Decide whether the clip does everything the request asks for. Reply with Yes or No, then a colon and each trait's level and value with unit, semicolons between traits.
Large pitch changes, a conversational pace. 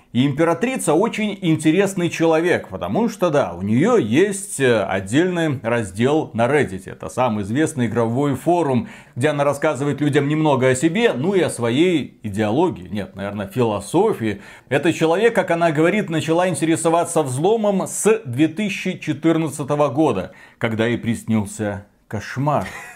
Yes: wide, 6.2 semitones; average, 130 wpm